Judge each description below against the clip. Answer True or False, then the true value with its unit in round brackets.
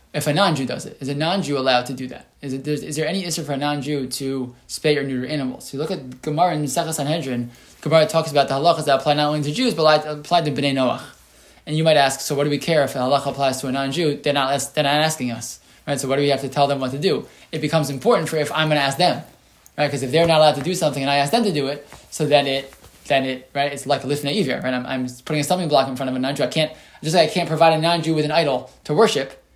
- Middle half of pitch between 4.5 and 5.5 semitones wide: False (2.6 semitones)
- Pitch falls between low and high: True (145 Hz)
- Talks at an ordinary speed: False (300 wpm)